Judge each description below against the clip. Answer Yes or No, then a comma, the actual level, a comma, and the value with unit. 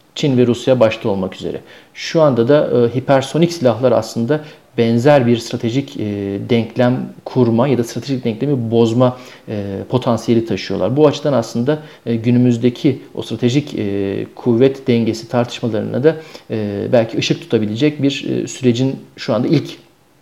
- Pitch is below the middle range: Yes, low, 120 Hz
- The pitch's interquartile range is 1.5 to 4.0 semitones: Yes, average, 3.3 semitones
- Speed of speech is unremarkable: No, fast, 145 wpm